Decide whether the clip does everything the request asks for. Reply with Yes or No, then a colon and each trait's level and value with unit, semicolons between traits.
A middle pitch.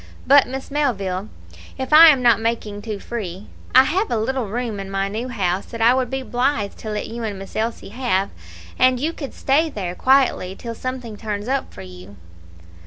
No: high, 230 Hz